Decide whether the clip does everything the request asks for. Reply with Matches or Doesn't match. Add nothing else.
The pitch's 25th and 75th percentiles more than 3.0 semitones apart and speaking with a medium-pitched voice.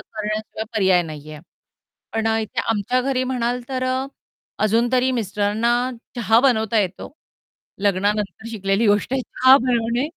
Doesn't match